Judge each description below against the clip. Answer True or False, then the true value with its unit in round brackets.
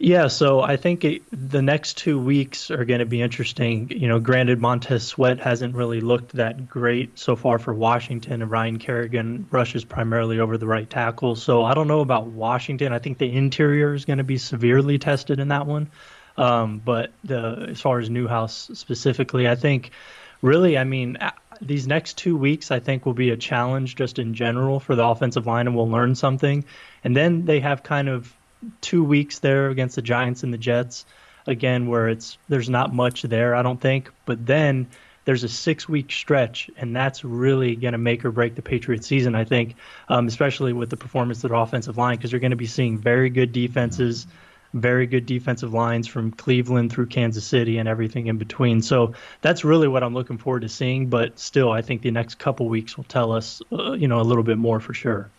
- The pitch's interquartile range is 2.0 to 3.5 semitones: True (2.5 semitones)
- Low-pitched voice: True (125 Hz)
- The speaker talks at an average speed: False (210 wpm)